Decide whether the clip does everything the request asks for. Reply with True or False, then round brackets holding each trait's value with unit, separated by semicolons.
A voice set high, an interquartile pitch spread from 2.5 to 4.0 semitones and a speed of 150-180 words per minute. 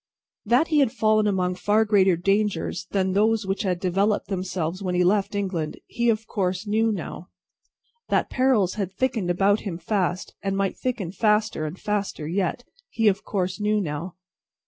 True (195 Hz; 2.8 semitones; 170 wpm)